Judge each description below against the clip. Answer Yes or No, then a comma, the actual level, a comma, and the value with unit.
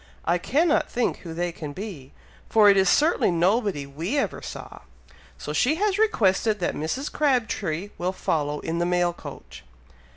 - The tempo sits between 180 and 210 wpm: No, average, 165 wpm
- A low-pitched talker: No, high, 190 Hz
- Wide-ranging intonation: Yes, wide, 6.6 semitones